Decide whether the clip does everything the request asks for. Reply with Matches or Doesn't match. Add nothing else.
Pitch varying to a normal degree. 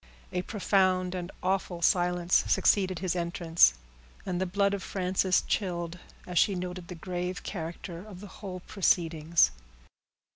Doesn't match